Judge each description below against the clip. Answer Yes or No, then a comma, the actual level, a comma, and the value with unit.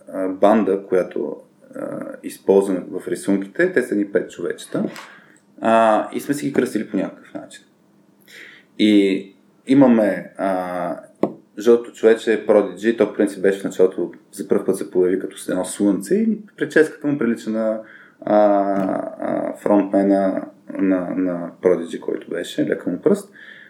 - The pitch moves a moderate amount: Yes, average, 3.1 semitones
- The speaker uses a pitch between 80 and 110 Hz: Yes, low, 100 Hz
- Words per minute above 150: No, average, 145 wpm